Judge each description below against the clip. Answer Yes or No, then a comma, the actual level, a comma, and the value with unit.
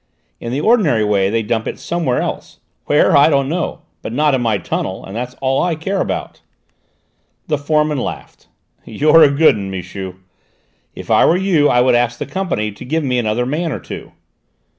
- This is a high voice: No, low, 135 Hz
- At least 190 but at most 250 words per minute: Yes, average, 195 wpm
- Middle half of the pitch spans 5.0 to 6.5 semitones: Yes, wide, 5.5 semitones